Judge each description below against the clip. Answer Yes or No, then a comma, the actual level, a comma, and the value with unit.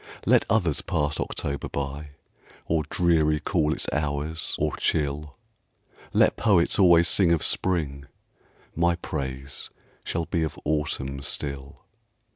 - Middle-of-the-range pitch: No, very low, 75 Hz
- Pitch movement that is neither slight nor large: Yes, average, 3.1 semitones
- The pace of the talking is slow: Yes, slow, 120 wpm